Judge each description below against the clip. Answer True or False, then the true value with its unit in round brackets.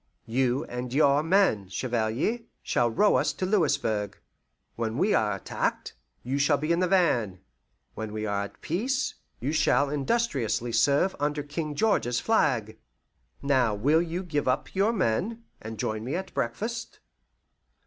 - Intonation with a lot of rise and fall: True (7.5 semitones)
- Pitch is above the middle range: False (140 Hz)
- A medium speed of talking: True (150 wpm)